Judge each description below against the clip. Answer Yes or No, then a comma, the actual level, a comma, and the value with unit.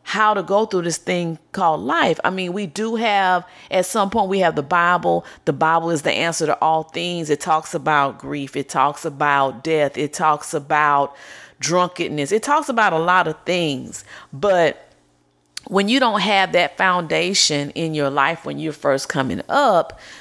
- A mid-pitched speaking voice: Yes, medium, 165 Hz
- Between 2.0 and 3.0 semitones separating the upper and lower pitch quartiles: No, average, 4.1 semitones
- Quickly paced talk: No, average, 185 wpm